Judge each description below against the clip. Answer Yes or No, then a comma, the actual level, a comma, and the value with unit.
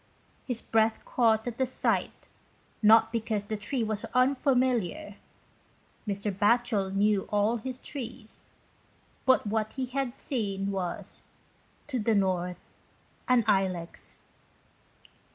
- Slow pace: Yes, slow, 115 wpm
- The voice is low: No, high, 220 Hz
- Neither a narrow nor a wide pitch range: Yes, average, 3.5 semitones